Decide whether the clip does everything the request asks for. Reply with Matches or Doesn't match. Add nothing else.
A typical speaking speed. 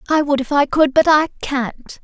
Doesn't match